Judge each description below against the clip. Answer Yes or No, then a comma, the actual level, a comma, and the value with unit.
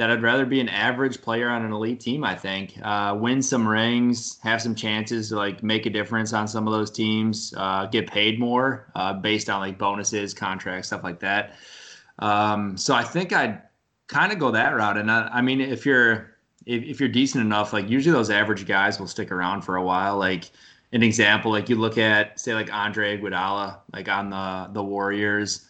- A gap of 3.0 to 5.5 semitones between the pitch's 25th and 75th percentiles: No, narrow, 2.6 semitones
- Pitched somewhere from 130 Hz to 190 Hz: No, low, 105 Hz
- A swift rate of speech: Yes, fast, 210 wpm